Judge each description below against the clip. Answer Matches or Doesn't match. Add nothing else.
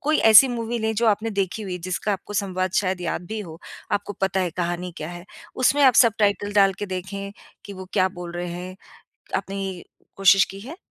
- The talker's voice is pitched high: Matches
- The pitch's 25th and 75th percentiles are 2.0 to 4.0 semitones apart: Matches